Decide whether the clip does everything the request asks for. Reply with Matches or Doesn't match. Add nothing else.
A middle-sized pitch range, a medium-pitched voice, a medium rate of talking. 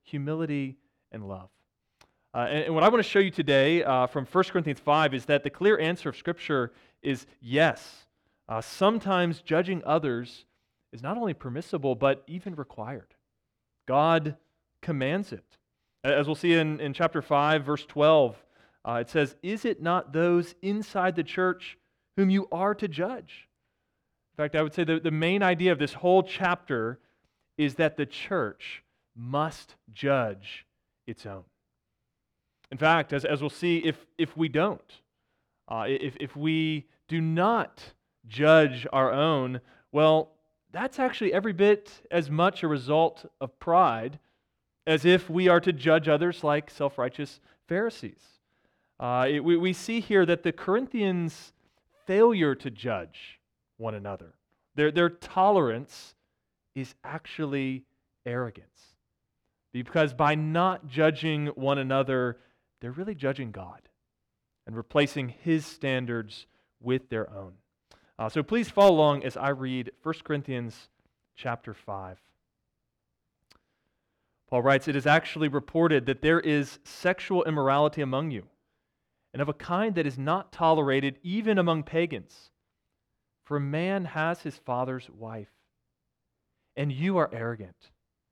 Matches